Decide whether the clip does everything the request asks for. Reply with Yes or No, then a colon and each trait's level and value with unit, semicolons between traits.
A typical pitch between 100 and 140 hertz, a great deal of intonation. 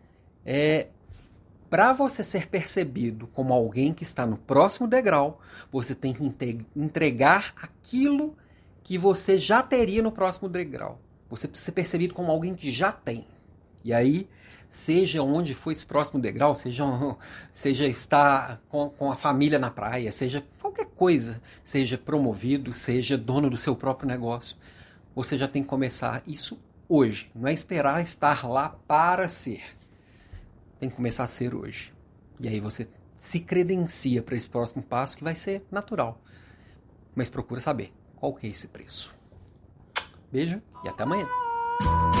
Yes: low, 135 Hz; wide, 5.8 semitones